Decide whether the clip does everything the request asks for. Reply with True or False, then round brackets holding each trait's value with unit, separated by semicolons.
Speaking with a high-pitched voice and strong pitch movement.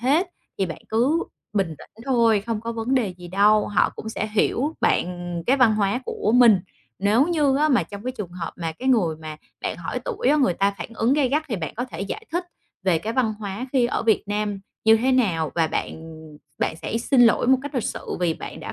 False (225 Hz; 4.8 semitones)